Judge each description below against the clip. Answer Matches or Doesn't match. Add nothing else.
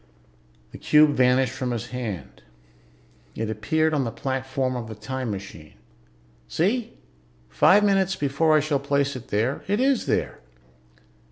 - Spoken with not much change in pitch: Doesn't match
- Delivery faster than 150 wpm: Doesn't match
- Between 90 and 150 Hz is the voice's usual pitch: Matches